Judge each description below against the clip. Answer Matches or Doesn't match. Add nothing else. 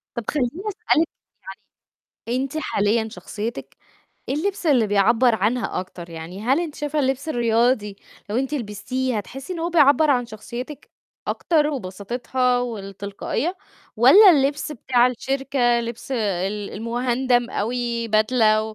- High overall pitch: Matches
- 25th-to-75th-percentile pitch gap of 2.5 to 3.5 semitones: Doesn't match